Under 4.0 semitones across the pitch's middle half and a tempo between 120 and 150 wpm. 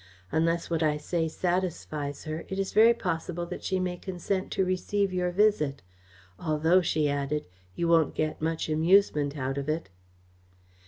No: average, 3.2 semitones; average, 160 wpm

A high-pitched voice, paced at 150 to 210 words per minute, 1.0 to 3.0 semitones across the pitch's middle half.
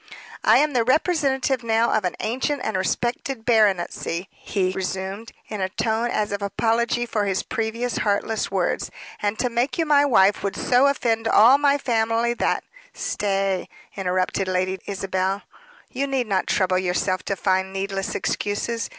No: high, 215 Hz; average, 160 wpm; average, 3.9 semitones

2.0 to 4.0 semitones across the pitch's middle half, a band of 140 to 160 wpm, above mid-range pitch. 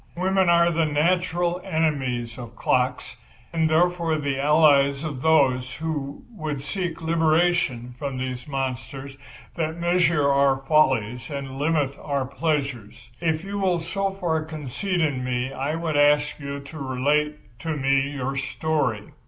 No: average, 3.4 semitones; average, 145 wpm; medium, 150 Hz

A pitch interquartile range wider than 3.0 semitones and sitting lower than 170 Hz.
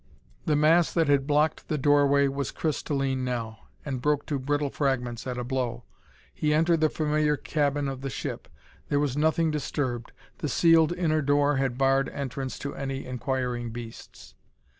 No: narrow, 2.4 semitones; medium, 140 Hz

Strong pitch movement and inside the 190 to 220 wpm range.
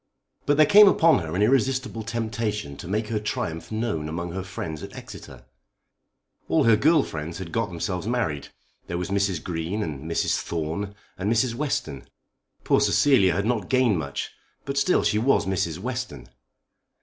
No: wide, 6.0 semitones; average, 170 wpm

